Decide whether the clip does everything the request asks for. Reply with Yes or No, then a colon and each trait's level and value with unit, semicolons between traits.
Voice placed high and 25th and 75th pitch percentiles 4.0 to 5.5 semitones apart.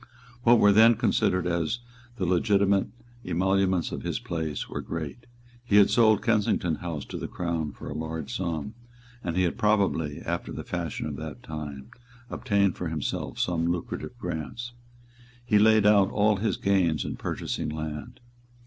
No: very low, 90 Hz; average, 4.4 semitones